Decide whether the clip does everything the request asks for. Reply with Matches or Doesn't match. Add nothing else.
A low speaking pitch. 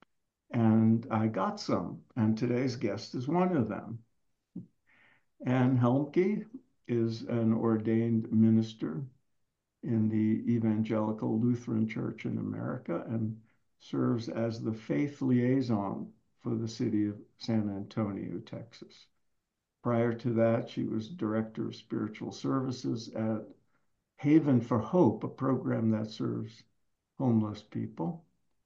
Matches